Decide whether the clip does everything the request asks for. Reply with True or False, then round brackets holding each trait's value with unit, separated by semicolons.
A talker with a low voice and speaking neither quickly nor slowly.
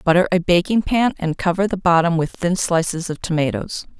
False (175 Hz; 195 wpm)